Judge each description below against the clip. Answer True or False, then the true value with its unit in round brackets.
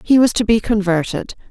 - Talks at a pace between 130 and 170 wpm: False (200 wpm)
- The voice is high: True (215 Hz)